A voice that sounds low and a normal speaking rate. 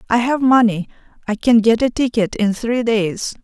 No: high, 235 Hz; average, 190 wpm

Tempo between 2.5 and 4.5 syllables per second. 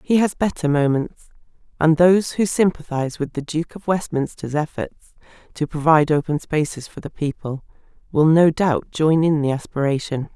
No: 5.2 syllables/s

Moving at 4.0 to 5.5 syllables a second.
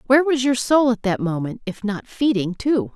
Yes: 5.1 syllables/s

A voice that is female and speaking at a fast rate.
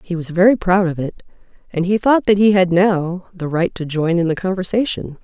Yes: female; fast, 230 wpm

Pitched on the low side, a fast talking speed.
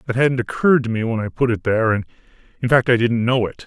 Yes: low, 120 Hz; fast, 280 wpm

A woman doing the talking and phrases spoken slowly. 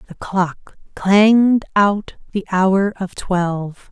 Yes: female; slow, 125 wpm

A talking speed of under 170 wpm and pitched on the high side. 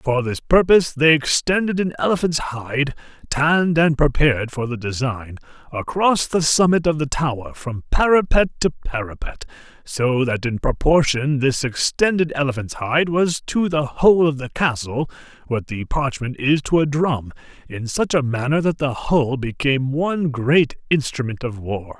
No: average, 160 wpm; medium, 140 Hz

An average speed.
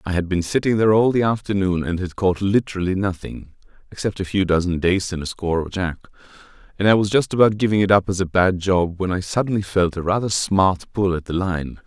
No: fast, 230 wpm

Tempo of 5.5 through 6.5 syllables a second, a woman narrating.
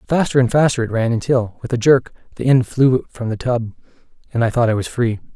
No: 5.7 syllables/s; male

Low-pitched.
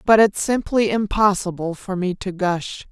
No: high, 195 Hz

